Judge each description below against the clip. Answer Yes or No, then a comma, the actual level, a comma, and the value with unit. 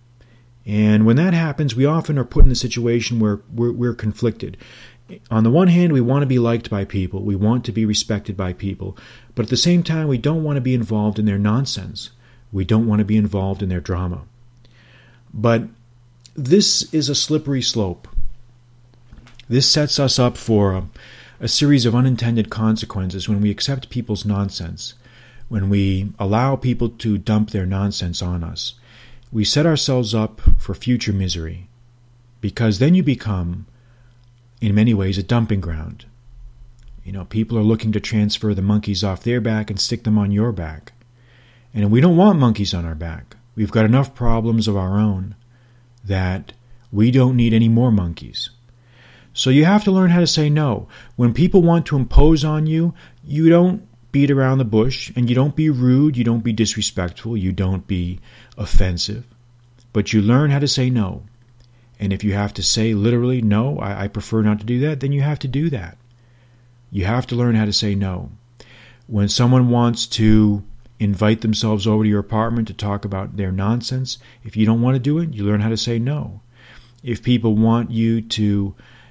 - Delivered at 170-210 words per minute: Yes, average, 185 wpm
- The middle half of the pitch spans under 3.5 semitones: Yes, average, 3.0 semitones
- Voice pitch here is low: Yes, low, 115 Hz